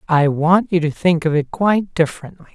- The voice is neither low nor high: Yes, medium, 170 Hz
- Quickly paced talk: Yes, fast, 215 wpm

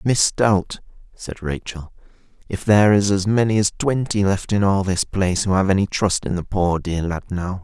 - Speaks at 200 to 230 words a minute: Yes, fast, 205 wpm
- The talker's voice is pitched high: No, very low, 95 Hz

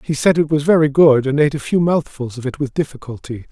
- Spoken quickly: Yes, fast, 255 wpm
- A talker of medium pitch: Yes, medium, 145 Hz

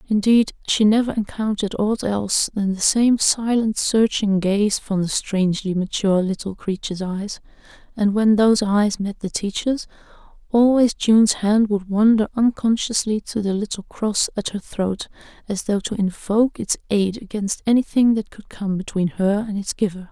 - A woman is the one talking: Yes, female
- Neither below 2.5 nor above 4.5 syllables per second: No, 4.8 syllables/s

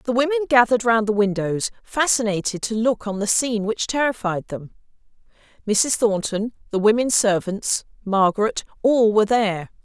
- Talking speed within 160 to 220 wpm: No, average, 140 wpm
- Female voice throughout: Yes, female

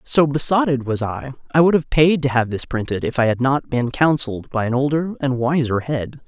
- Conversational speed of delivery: No, fast, 230 wpm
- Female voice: Yes, female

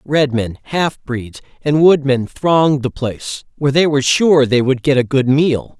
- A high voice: No, medium, 140 Hz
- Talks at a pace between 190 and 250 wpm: Yes, fast, 205 wpm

